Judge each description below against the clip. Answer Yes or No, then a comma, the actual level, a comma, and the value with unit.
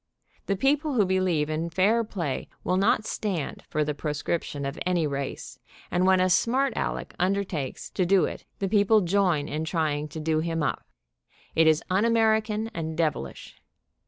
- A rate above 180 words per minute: No, average, 170 wpm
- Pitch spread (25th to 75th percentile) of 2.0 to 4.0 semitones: No, average, 4.5 semitones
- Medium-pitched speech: Yes, medium, 180 Hz